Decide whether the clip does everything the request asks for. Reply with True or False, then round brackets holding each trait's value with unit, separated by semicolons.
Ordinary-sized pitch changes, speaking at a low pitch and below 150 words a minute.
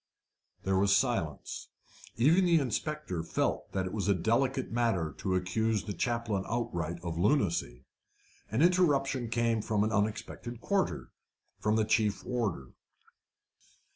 True (4.4 semitones; 110 Hz; 135 wpm)